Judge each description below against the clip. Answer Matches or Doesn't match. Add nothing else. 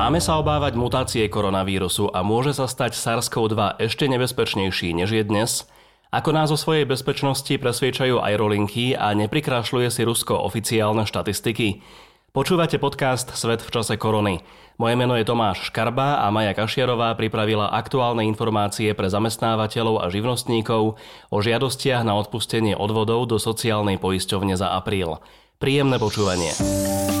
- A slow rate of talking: Doesn't match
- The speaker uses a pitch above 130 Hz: Doesn't match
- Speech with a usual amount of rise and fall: Matches